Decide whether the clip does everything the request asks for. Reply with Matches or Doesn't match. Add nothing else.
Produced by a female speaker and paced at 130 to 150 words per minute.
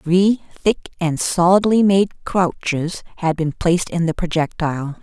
Matches